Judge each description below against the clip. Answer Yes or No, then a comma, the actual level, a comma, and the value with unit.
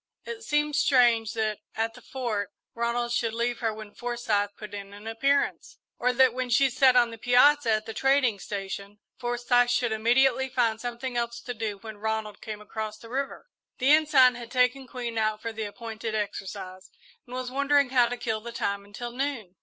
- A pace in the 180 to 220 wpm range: Yes, average, 195 wpm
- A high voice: Yes, high, 235 Hz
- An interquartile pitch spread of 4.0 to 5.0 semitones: No, average, 2.7 semitones